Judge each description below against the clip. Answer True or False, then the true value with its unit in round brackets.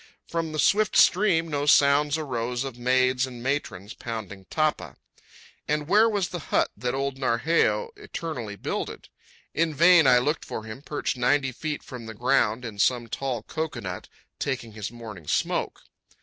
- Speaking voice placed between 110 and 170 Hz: True (135 Hz)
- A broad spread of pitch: False (5.0 semitones)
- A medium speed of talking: True (160 wpm)